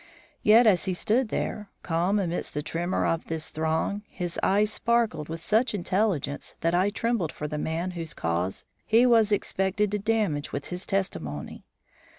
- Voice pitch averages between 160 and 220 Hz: Yes, medium, 185 Hz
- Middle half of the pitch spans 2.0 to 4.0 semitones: No, average, 4.7 semitones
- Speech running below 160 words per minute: No, average, 165 wpm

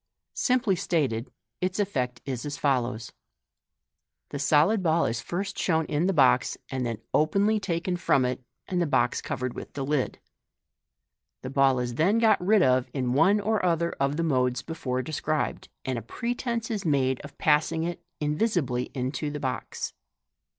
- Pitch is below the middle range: No, medium, 150 Hz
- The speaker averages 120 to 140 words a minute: No, average, 175 wpm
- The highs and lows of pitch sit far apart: Yes, wide, 6.0 semitones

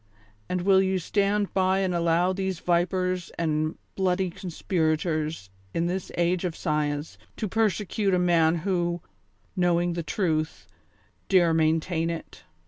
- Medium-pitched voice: Yes, medium, 175 Hz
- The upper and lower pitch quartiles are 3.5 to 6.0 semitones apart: No, narrow, 2.4 semitones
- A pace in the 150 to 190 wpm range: No, slow, 135 wpm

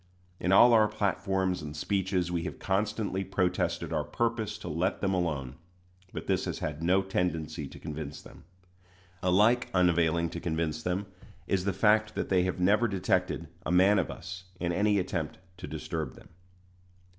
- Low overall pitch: Yes, very low, 90 Hz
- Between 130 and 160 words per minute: No, average, 170 wpm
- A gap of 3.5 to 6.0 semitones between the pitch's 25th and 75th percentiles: No, average, 3.0 semitones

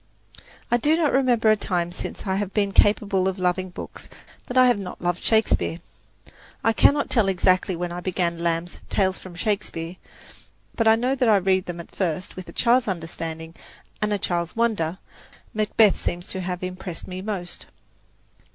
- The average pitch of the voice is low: No, high, 190 Hz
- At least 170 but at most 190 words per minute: Yes, average, 180 wpm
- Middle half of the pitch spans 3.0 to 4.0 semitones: Yes, average, 3.7 semitones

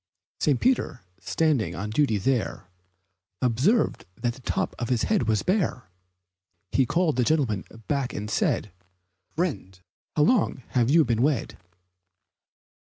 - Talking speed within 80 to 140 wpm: Yes, slow, 135 wpm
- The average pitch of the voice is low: Yes, low, 130 Hz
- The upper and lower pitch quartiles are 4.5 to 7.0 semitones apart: Yes, wide, 5.5 semitones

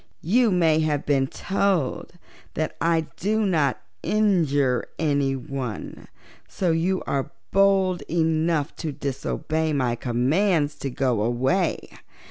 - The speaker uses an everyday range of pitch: Yes, average, 5.0 semitones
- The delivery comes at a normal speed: No, slow, 110 wpm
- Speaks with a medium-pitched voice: Yes, medium, 155 Hz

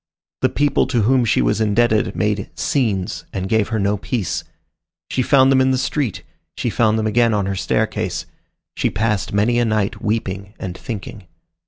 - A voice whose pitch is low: Yes, low, 110 Hz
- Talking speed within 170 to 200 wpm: Yes, average, 180 wpm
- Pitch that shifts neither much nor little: Yes, average, 3.3 semitones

